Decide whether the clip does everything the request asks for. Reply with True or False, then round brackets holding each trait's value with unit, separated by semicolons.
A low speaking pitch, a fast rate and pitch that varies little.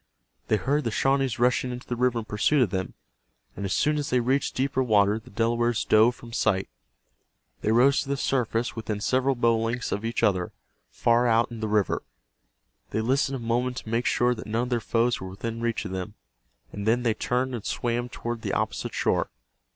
True (120 Hz; 210 wpm; 2.3 semitones)